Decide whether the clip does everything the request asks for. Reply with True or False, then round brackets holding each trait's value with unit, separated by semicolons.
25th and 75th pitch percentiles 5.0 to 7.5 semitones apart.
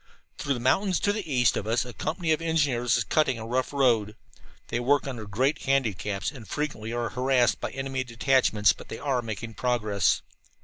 False (3.6 semitones)